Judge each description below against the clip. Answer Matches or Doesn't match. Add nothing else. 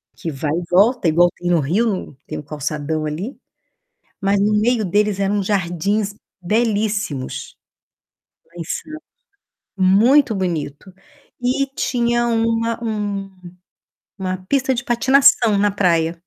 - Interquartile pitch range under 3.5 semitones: Doesn't match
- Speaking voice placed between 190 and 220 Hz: Matches